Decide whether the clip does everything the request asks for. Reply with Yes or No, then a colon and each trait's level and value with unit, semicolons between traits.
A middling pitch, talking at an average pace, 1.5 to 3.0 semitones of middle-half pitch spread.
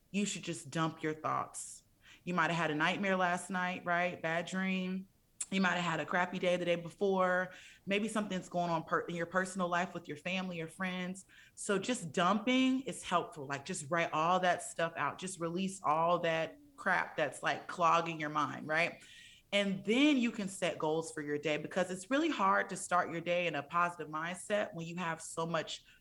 No: medium, 175 Hz; fast, 210 wpm; narrow, 2.4 semitones